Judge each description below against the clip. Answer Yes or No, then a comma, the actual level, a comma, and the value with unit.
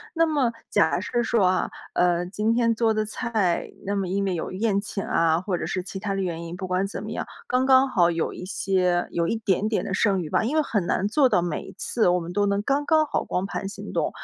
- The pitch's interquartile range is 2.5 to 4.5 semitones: Yes, average, 4.1 semitones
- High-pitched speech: Yes, high, 200 Hz